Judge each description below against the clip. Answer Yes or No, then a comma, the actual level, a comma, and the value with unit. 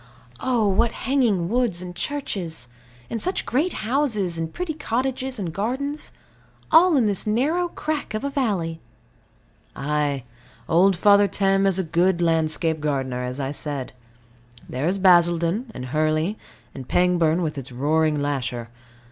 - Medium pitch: Yes, medium, 180 Hz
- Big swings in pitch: Yes, wide, 7.3 semitones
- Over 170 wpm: No, average, 145 wpm